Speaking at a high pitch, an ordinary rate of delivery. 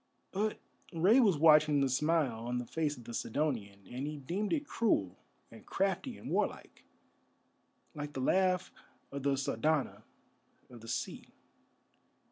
No: medium, 150 Hz; average, 145 wpm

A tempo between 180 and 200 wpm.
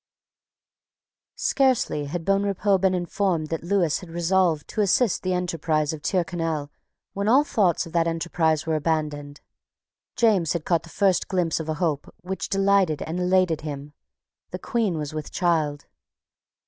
No: average, 150 wpm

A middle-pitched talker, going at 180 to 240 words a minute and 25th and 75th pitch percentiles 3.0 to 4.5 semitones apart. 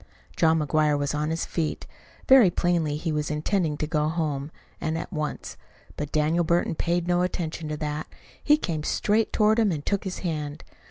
No: medium, 160 Hz; average, 185 wpm; narrow, 2.6 semitones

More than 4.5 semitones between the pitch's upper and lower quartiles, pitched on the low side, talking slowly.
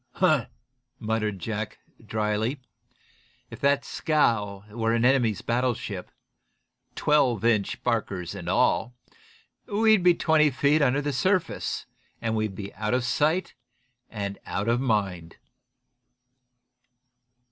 Yes: average, 5.0 semitones; low, 115 Hz; slow, 115 wpm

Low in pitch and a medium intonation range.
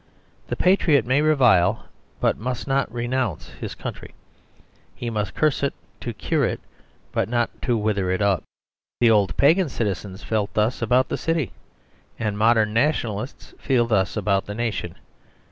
Yes: low, 115 Hz; average, 3.9 semitones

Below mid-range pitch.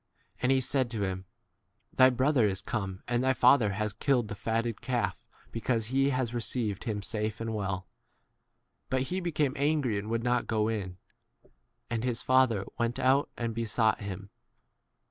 Yes: low, 115 Hz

